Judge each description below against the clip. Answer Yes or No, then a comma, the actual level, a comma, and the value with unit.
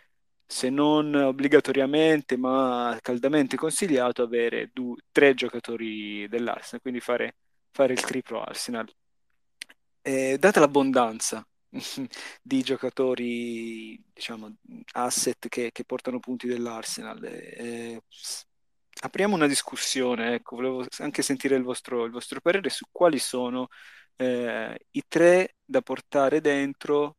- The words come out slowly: Yes, slow, 110 wpm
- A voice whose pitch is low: Yes, low, 130 Hz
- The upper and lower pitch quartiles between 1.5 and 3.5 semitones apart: Yes, average, 2.7 semitones